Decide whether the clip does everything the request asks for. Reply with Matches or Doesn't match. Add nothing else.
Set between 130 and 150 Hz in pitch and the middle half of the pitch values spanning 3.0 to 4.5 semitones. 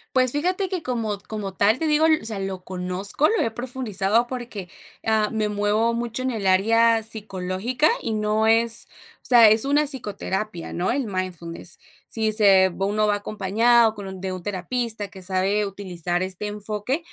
Doesn't match